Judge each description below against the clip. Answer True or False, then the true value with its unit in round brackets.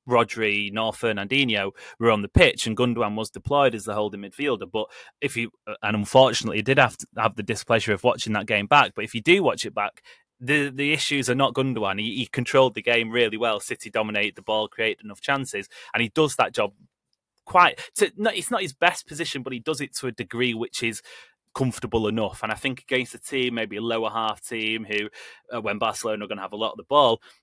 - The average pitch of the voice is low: True (115 Hz)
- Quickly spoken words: True (230 wpm)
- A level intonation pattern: False (3.7 semitones)